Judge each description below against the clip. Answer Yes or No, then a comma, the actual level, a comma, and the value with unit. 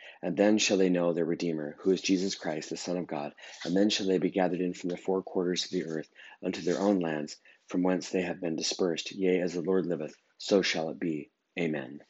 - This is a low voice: Yes, very low, 90 Hz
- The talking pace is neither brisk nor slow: No, fast, 245 wpm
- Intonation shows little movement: Yes, narrow, 1.7 semitones